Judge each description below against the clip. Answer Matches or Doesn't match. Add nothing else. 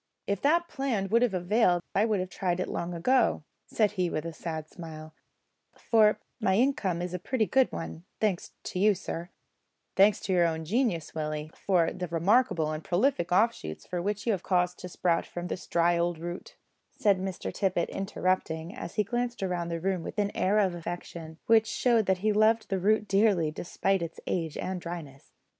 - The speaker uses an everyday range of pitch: Matches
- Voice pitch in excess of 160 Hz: Matches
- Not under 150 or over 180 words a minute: Doesn't match